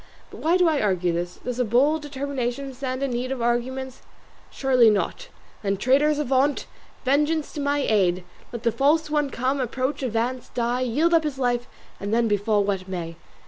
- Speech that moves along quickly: No, average, 185 wpm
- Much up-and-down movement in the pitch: No, average, 3.7 semitones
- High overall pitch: Yes, very high, 255 Hz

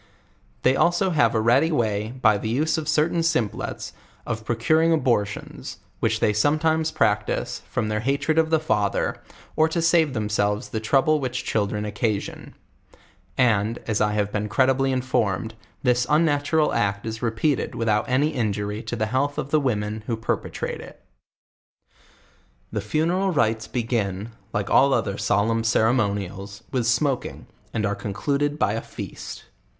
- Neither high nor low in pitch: No, low, 120 Hz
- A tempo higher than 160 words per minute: No, average, 155 wpm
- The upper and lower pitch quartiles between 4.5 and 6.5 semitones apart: Yes, wide, 5.5 semitones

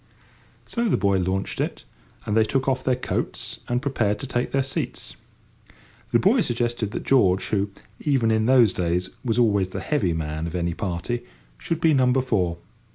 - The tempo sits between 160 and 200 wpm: Yes, average, 180 wpm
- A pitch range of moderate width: No, wide, 5.7 semitones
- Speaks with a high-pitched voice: No, low, 110 Hz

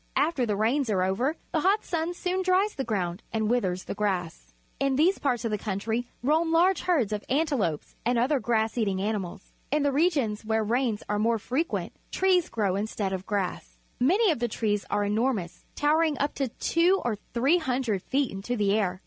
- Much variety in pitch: Yes, wide, 6.4 semitones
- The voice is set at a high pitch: Yes, high, 235 Hz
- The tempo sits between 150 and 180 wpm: No, average, 190 wpm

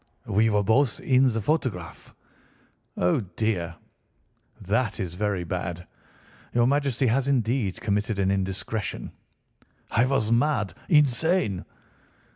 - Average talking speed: No, slow, 105 wpm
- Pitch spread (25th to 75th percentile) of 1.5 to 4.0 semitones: No, average, 5.1 semitones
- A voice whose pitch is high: No, low, 110 Hz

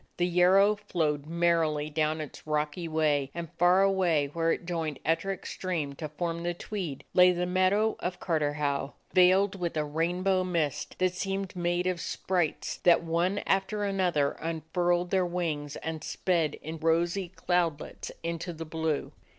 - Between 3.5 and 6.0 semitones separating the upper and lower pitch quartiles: No, average, 2.7 semitones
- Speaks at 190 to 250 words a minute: No, average, 155 wpm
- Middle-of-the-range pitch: Yes, medium, 170 Hz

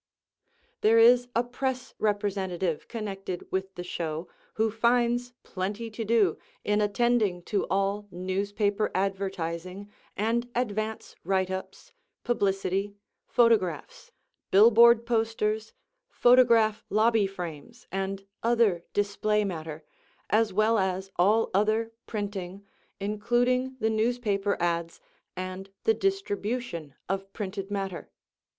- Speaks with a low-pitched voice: No, high, 205 Hz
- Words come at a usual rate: No, slow, 105 wpm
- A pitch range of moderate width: Yes, average, 3.1 semitones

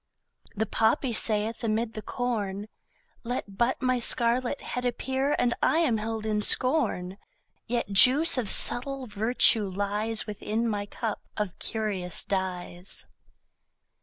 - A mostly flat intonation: No, average, 3.2 semitones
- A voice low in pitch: No, high, 220 Hz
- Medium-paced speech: No, slow, 130 wpm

